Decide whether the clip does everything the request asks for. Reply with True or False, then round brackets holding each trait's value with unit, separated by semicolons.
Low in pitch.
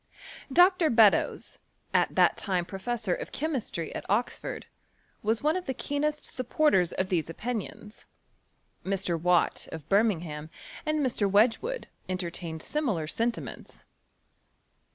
False (210 Hz)